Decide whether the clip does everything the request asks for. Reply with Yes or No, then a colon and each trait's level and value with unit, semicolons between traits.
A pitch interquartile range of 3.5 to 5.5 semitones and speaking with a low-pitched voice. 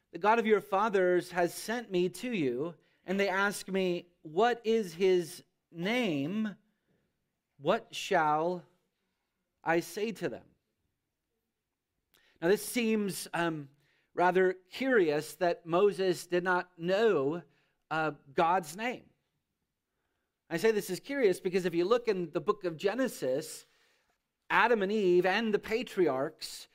No: average, 3.8 semitones; medium, 185 Hz